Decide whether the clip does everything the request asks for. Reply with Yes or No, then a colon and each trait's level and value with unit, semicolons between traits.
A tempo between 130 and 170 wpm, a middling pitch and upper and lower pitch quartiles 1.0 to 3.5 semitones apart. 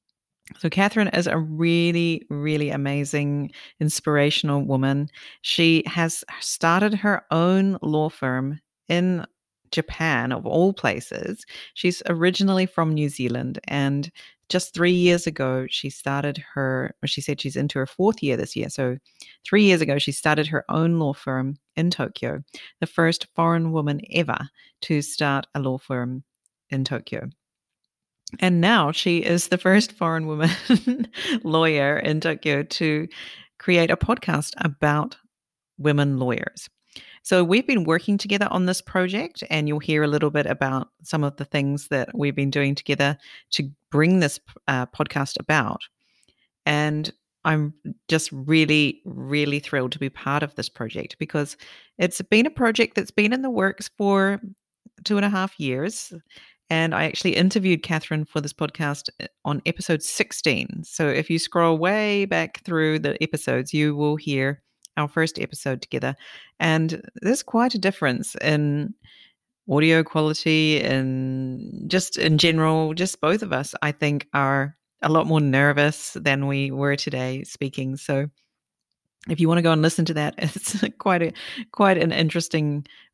No: average, 155 wpm; medium, 155 Hz; average, 3.9 semitones